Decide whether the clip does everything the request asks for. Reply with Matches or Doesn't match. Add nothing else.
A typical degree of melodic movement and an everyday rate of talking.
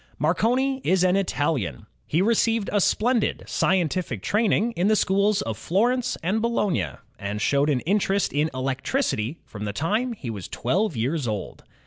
Doesn't match